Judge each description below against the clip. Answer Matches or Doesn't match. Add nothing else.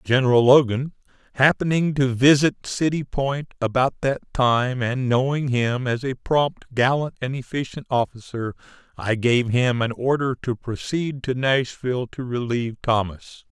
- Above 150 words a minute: Doesn't match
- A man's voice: Matches